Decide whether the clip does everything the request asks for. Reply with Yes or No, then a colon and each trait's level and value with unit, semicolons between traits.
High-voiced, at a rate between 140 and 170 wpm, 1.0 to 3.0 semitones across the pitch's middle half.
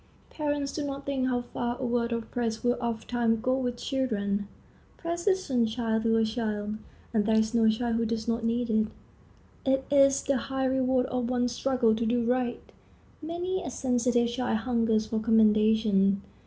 No: high, 240 Hz; average, 180 wpm; narrow, 2.6 semitones